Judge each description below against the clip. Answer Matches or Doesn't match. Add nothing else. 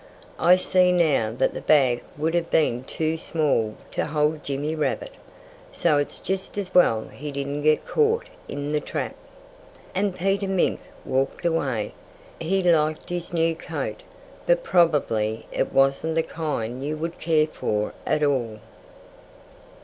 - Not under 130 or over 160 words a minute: Matches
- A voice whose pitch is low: Doesn't match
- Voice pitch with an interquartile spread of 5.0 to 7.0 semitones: Doesn't match